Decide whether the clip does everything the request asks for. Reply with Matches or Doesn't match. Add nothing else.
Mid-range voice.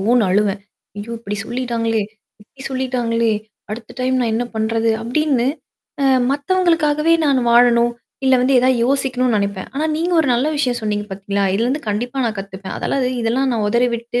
Doesn't match